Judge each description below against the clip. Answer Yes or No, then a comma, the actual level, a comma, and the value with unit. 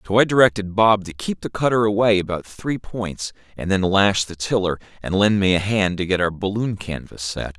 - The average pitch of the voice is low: Yes, low, 100 Hz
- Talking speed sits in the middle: No, fast, 220 wpm